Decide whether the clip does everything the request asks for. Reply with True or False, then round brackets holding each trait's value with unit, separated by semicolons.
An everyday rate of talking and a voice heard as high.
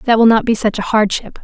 False (295 wpm; 215 Hz)